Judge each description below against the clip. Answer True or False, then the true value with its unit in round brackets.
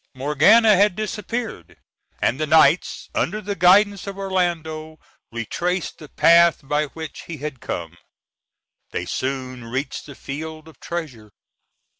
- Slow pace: True (130 wpm)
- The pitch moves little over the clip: False (5.3 semitones)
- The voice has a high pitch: False (160 Hz)